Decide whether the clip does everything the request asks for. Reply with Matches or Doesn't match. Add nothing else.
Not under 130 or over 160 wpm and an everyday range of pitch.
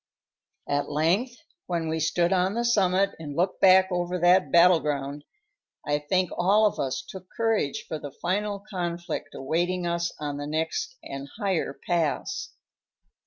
Matches